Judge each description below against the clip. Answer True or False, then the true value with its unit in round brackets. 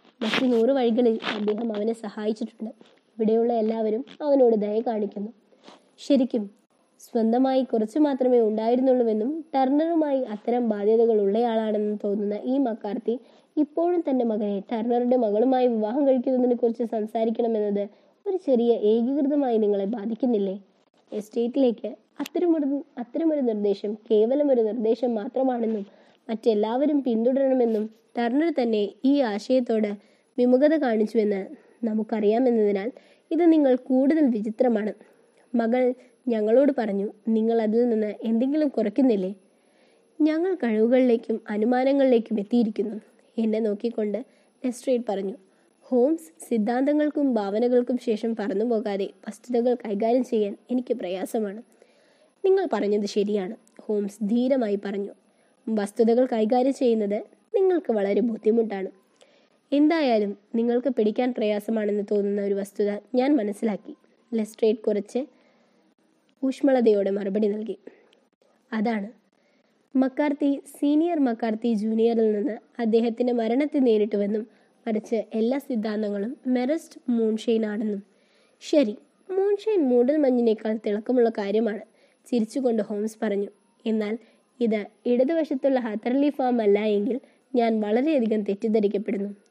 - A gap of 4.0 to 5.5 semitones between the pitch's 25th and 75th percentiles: False (3.2 semitones)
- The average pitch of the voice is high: True (230 Hz)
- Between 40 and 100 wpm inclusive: True (95 wpm)